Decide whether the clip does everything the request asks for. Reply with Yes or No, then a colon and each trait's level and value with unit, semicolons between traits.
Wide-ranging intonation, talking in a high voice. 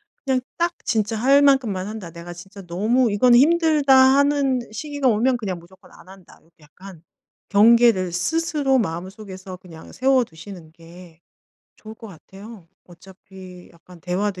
Yes: wide, 6.3 semitones; high, 200 Hz